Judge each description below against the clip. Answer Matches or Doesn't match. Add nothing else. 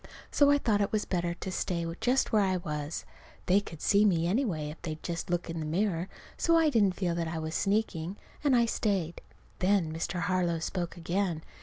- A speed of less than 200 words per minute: Doesn't match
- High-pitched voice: Doesn't match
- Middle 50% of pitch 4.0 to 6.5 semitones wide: Doesn't match